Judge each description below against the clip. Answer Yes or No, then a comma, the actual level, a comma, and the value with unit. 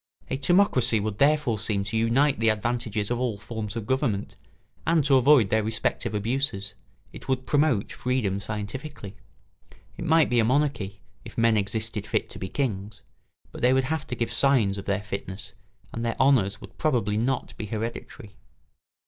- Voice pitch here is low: Yes, low, 115 Hz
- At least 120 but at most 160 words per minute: No, average, 175 wpm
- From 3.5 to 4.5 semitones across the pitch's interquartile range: Yes, average, 4.2 semitones